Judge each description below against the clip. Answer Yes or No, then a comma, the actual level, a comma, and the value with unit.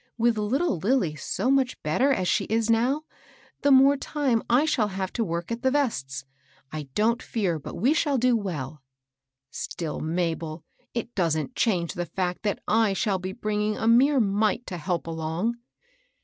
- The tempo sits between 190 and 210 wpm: No, average, 175 wpm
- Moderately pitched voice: No, high, 210 Hz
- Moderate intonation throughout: No, wide, 6.2 semitones